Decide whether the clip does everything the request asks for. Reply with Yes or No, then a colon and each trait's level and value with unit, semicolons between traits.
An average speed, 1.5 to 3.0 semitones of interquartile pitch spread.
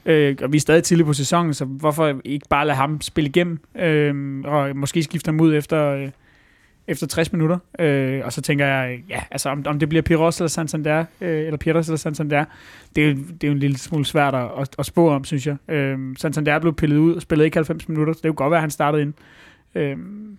No: fast, 245 wpm; narrow, 2.4 semitones